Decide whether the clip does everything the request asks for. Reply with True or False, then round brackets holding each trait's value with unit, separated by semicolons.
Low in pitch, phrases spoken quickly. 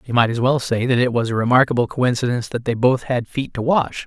True (125 Hz; 265 wpm)